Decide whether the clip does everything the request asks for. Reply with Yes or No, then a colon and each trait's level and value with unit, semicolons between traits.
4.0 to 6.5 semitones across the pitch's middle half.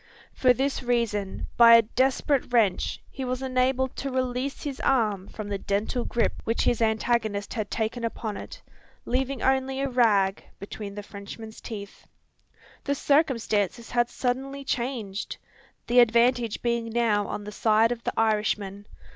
No: average, 3.4 semitones